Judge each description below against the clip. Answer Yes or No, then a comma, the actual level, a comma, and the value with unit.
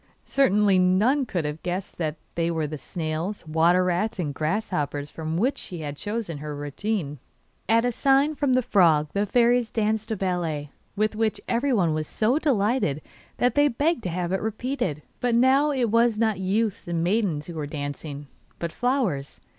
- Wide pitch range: Yes, wide, 6.6 semitones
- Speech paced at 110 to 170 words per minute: No, average, 180 wpm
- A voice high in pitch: Yes, high, 195 Hz